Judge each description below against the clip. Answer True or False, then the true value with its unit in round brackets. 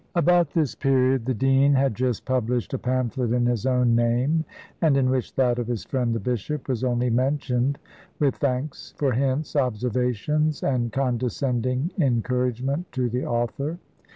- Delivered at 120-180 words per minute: True (155 wpm)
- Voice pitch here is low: True (130 Hz)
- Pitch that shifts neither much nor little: False (2.2 semitones)